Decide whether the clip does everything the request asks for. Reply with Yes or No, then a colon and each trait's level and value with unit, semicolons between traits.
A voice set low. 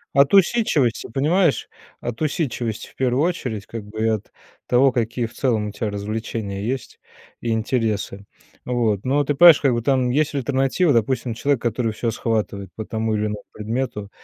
Yes: low, 120 Hz